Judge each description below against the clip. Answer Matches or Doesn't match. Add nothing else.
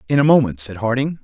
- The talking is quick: Matches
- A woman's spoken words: Doesn't match